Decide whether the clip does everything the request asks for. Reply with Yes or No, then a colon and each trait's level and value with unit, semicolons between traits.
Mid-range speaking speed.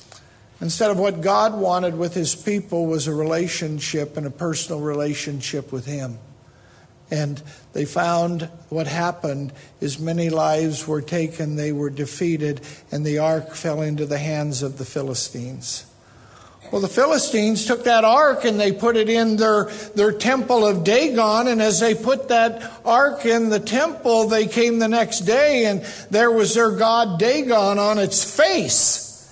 Yes: average, 160 wpm